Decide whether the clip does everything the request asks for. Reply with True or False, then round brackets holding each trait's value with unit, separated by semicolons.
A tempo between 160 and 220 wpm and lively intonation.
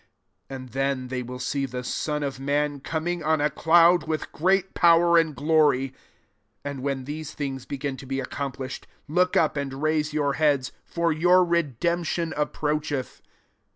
False (165 wpm; 3.2 semitones)